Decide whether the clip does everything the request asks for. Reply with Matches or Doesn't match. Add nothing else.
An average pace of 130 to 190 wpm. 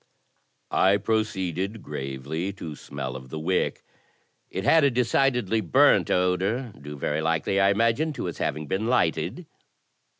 Matches